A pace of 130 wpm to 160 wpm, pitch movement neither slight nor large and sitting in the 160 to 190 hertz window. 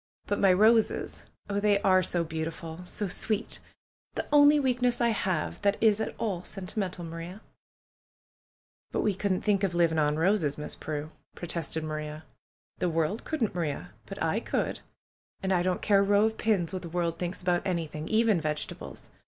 No: average, 175 wpm; average, 4.1 semitones; medium, 185 Hz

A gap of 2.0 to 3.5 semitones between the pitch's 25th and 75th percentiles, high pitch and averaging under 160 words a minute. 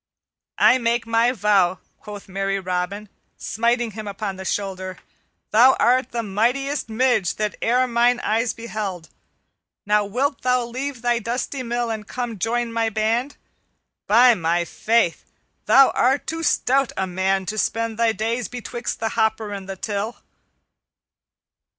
Yes: average, 3.1 semitones; high, 225 Hz; average, 150 wpm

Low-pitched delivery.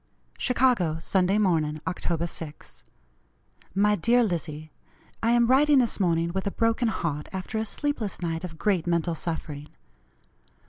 No: medium, 180 Hz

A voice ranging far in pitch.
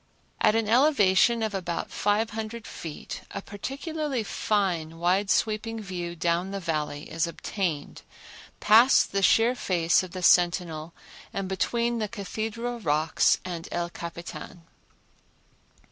No: average, 4.5 semitones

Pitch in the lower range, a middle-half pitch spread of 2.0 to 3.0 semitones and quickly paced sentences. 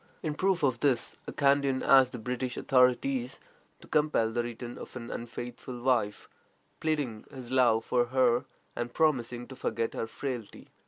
No: low, 125 Hz; narrow, 2.5 semitones; average, 160 wpm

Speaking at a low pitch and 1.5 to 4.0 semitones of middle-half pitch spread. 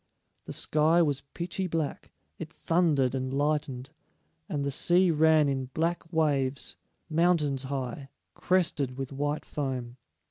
No: medium, 145 Hz; average, 3.4 semitones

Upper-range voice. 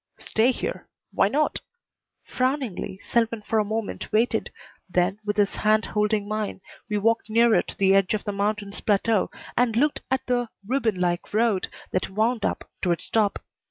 Yes: high, 215 Hz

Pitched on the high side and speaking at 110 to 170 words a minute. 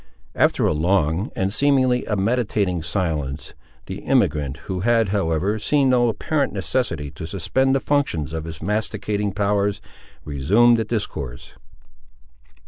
No: low, 100 Hz; slow, 135 wpm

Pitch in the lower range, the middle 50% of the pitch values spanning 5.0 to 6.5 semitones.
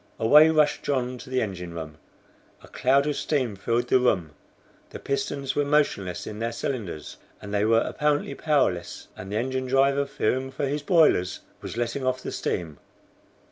Yes: low, 130 Hz; wide, 5.4 semitones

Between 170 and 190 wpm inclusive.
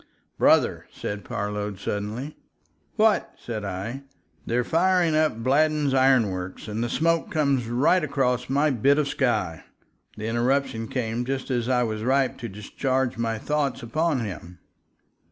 No: average, 150 wpm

